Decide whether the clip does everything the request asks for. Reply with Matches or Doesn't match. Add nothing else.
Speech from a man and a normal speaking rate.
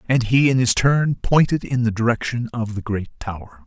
Doesn't match